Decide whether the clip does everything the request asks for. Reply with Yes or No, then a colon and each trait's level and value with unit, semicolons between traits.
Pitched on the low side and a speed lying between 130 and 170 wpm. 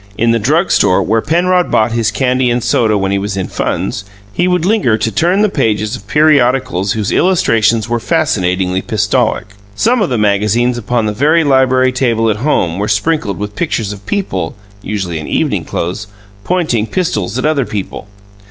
No: low, 115 Hz; average, 180 wpm